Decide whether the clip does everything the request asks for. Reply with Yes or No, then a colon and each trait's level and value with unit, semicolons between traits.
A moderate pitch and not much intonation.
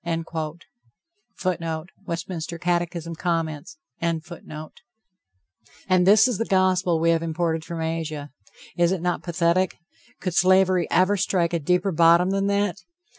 Yes: medium, 170 Hz; narrow, 2.3 semitones